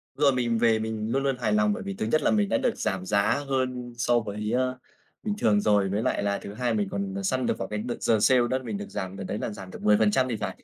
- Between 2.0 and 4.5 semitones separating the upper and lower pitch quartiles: Yes, average, 3.7 semitones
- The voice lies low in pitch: Yes, low, 110 Hz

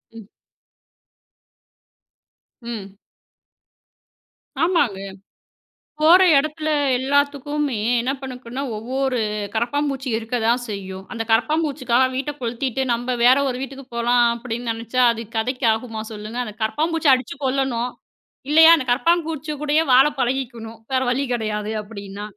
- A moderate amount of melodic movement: Yes, average, 3.6 semitones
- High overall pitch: Yes, very high, 250 Hz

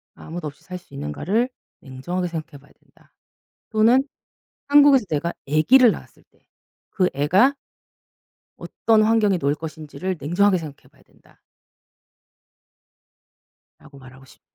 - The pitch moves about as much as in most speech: No, wide, 6.7 semitones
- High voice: No, medium, 175 Hz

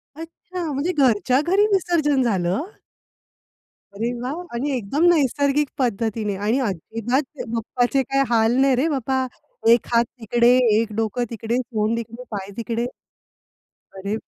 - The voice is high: Yes, high, 240 Hz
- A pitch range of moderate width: Yes, average, 3.7 semitones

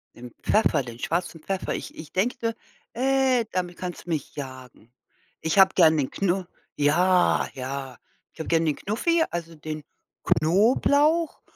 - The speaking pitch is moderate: Yes, medium, 175 Hz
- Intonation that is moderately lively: No, wide, 6.0 semitones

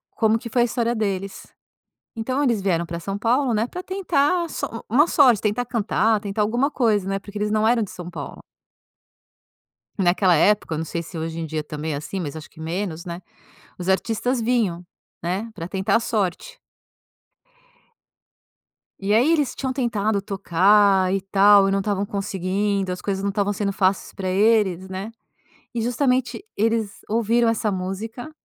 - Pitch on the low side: No, high, 205 Hz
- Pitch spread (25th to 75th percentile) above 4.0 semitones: No, average, 3.5 semitones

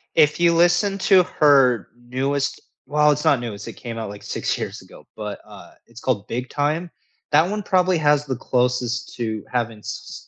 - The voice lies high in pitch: No, low, 135 Hz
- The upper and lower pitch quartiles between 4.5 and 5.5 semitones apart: Yes, average, 4.9 semitones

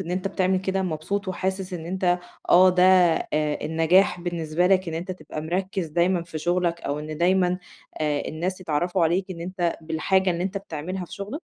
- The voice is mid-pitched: Yes, medium, 180 Hz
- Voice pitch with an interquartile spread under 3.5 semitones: Yes, narrow, 2.5 semitones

